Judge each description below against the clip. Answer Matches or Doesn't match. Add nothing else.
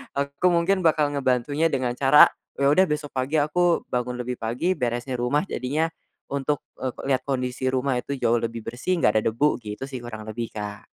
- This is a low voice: Matches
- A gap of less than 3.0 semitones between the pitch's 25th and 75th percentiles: Doesn't match